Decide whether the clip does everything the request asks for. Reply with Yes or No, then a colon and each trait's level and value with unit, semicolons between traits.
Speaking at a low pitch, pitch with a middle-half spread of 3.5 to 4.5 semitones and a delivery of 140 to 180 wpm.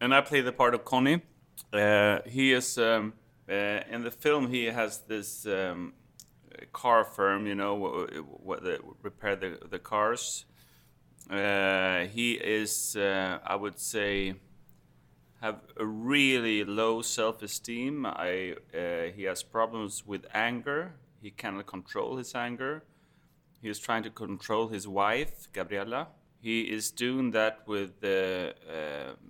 Yes: low, 110 Hz; average, 3.8 semitones; average, 145 wpm